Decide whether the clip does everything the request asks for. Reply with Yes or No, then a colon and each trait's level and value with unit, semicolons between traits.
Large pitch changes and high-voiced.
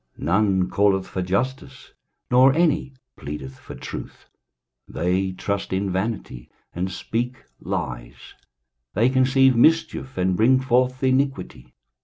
No: wide, 5.9 semitones; low, 110 Hz